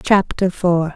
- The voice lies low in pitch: No, medium, 180 Hz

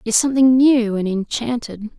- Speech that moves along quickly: No, average, 180 wpm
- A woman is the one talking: Yes, female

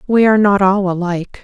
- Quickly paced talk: Yes, fast, 210 wpm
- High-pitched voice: Yes, high, 195 Hz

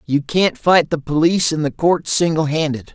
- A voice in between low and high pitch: Yes, medium, 155 Hz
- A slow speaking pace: No, fast, 205 wpm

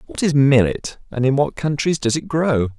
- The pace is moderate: No, fast, 215 wpm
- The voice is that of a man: Yes, male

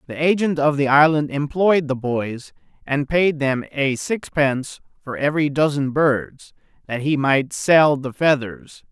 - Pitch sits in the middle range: Yes, medium, 145 Hz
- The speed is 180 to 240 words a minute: No, average, 155 wpm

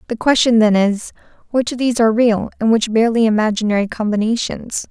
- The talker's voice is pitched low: No, high, 225 Hz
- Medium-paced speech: Yes, average, 170 wpm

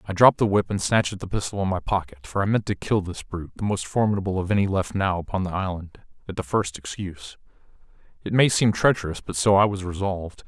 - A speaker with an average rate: No, fast, 240 wpm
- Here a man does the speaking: Yes, male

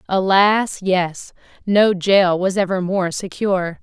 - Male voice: No, female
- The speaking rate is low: Yes, slow, 125 wpm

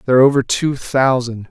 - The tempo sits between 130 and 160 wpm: No, average, 200 wpm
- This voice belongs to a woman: No, male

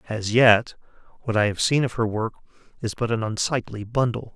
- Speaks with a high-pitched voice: No, low, 115 Hz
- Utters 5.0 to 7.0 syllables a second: Yes, 5.2 syllables/s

